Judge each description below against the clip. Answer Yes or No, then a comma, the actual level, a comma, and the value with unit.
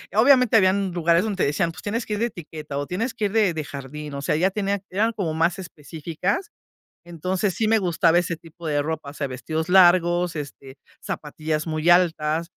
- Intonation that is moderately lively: Yes, average, 4.0 semitones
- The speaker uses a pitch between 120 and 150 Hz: No, medium, 170 Hz